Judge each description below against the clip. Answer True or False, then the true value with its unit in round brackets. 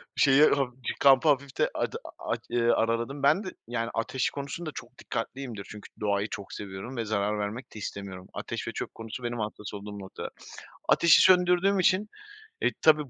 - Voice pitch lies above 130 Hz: False (120 Hz)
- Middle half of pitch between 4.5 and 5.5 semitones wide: True (5.1 semitones)